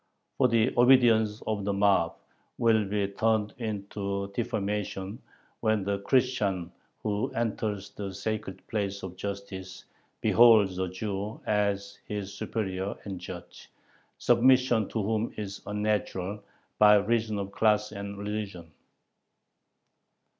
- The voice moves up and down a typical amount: No, narrow, 1.8 semitones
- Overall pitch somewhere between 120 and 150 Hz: No, low, 105 Hz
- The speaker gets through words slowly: Yes, slow, 120 wpm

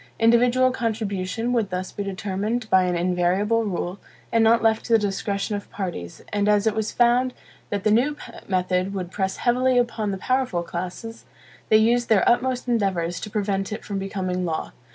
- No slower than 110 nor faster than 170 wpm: No, average, 180 wpm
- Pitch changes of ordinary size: Yes, average, 3.6 semitones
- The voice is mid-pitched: No, high, 205 Hz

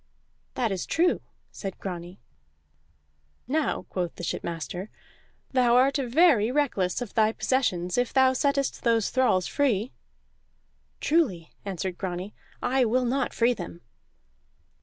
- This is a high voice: Yes, high, 235 Hz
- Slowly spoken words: Yes, slow, 120 wpm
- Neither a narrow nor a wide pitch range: No, wide, 6.0 semitones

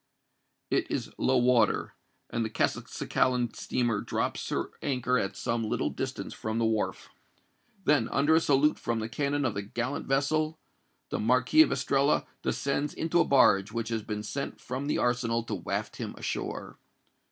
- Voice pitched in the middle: No, low, 125 Hz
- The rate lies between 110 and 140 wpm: No, average, 165 wpm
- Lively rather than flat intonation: No, average, 3.7 semitones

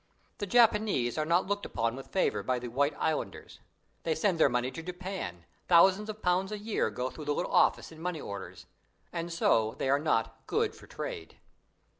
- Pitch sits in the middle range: Yes, medium, 160 Hz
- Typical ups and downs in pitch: No, wide, 7.2 semitones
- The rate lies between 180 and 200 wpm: Yes, average, 195 wpm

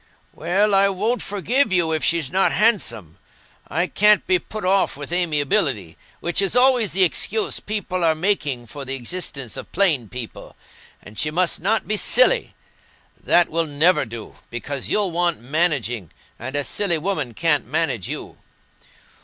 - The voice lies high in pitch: No, medium, 175 Hz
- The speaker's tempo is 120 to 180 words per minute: Yes, average, 160 wpm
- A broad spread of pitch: Yes, wide, 6.1 semitones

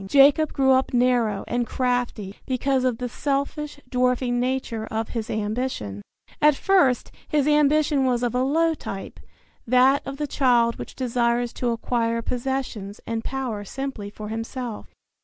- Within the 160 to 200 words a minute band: No, average, 150 wpm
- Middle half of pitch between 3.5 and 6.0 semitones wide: No, average, 2.8 semitones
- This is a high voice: Yes, very high, 250 Hz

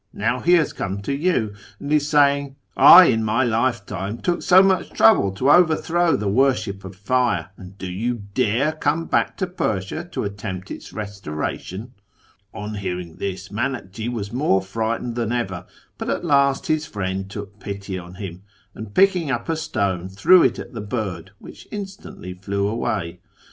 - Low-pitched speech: Yes, low, 110 Hz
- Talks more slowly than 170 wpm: No, average, 180 wpm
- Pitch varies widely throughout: Yes, wide, 6.2 semitones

